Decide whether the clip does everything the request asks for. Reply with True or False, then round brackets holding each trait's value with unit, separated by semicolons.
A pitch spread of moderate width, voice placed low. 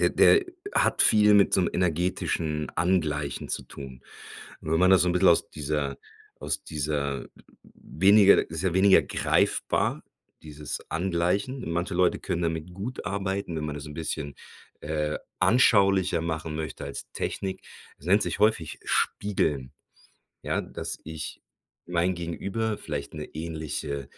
True (3.9 semitones; 85 Hz)